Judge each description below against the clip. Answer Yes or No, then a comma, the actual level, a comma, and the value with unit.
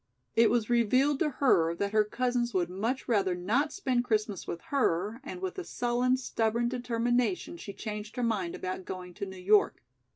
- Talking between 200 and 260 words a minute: No, average, 185 wpm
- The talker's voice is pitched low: No, high, 230 Hz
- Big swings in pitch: No, average, 4.0 semitones